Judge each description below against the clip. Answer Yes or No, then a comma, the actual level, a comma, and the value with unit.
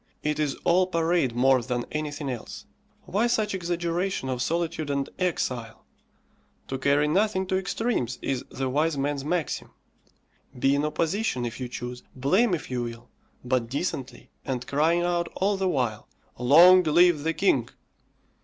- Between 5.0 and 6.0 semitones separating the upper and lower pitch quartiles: Yes, wide, 5.4 semitones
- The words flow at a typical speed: Yes, average, 155 wpm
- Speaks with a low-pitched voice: No, medium, 150 Hz